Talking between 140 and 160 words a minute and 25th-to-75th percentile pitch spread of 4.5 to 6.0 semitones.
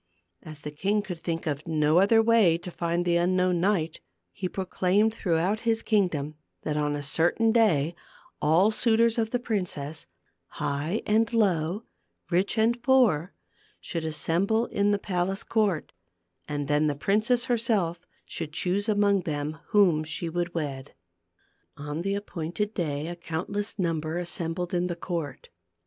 Yes: average, 155 wpm; average, 4.8 semitones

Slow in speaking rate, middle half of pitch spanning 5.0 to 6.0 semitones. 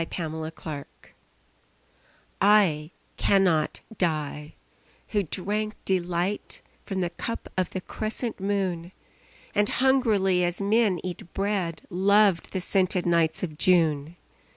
No: slow, 110 wpm; average, 3.3 semitones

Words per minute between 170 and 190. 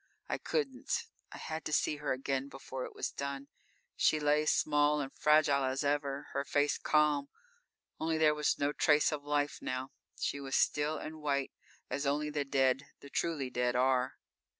Yes: average, 175 wpm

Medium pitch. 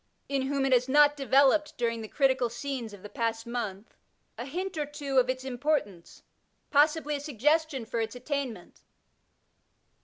No: very high, 265 Hz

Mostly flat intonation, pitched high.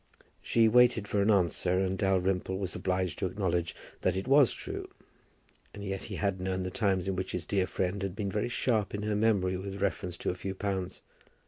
No: narrow, 1.8 semitones; very low, 95 Hz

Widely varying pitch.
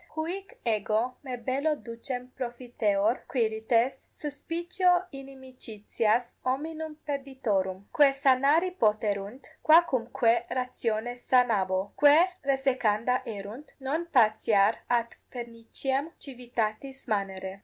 No: average, 4.0 semitones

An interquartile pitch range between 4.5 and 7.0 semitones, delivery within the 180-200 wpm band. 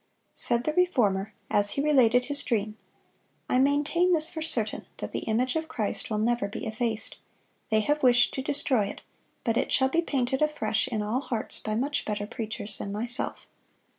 Yes: average, 4.8 semitones; average, 190 wpm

